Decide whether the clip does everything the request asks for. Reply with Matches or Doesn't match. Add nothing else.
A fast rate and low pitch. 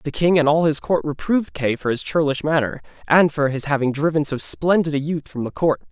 Doesn't match